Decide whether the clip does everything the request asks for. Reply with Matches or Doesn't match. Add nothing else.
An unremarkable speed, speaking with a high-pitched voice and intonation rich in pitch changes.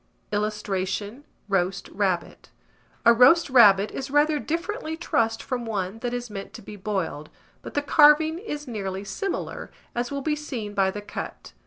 Matches